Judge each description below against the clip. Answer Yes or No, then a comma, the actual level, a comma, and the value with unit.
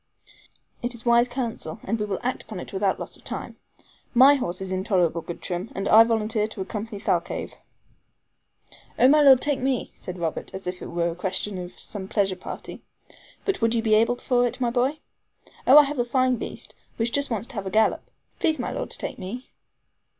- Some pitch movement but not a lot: Yes, average, 4.6 semitones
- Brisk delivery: Yes, fast, 215 wpm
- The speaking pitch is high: Yes, high, 225 Hz